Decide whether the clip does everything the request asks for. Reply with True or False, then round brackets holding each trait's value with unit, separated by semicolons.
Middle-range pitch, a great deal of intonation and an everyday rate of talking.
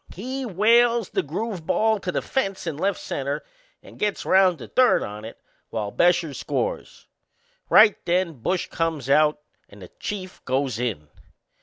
True (175 Hz; 7.1 semitones; 160 wpm)